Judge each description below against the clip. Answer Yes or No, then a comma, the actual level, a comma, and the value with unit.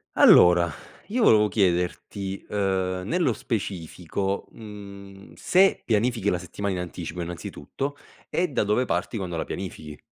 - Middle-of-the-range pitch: No, low, 100 Hz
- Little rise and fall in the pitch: No, average, 3.3 semitones